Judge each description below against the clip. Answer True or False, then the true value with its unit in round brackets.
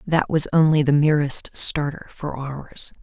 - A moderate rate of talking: True (160 wpm)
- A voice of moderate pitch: True (150 Hz)